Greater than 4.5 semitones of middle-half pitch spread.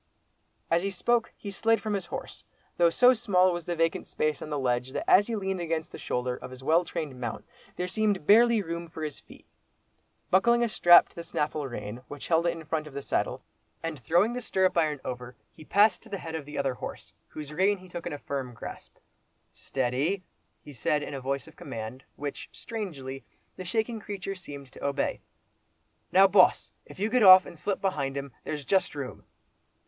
Yes: wide, 5.6 semitones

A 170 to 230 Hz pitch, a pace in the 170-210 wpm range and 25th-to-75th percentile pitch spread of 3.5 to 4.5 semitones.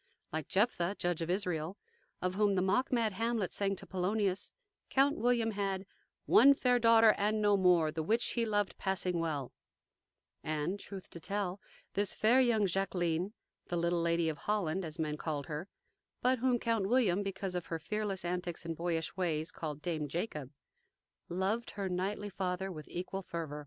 Yes: high, 190 Hz; average, 175 wpm; average, 3.8 semitones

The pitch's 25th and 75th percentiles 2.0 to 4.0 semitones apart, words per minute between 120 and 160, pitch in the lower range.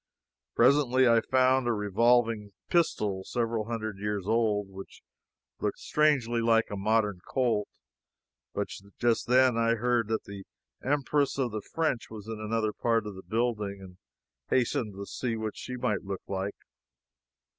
Yes: average, 3.0 semitones; average, 155 wpm; low, 115 Hz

